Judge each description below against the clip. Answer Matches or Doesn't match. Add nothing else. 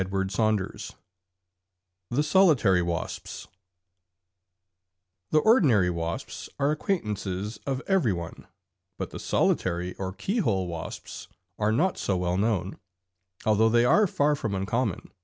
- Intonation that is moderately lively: Doesn't match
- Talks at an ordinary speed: Doesn't match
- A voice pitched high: Doesn't match